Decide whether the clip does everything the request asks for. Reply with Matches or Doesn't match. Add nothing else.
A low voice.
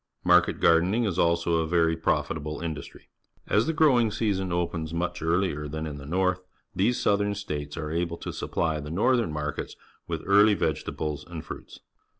Matches